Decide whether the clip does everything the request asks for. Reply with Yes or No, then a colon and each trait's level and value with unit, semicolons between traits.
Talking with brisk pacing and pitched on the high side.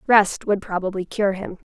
No: average, 175 wpm; high, 195 Hz